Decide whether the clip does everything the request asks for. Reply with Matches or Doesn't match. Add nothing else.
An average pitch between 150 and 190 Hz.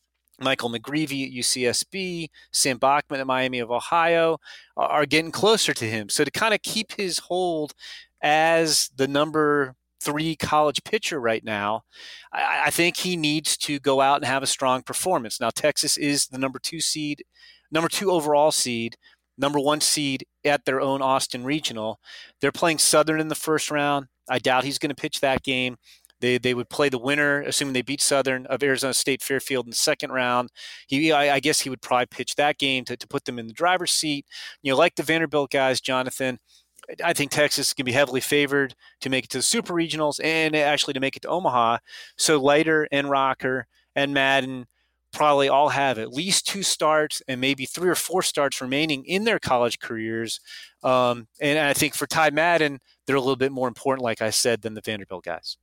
Doesn't match